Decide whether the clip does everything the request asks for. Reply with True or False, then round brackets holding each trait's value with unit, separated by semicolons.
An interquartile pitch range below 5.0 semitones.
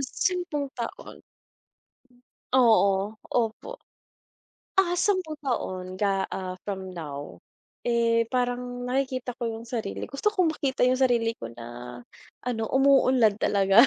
False (5.3 semitones)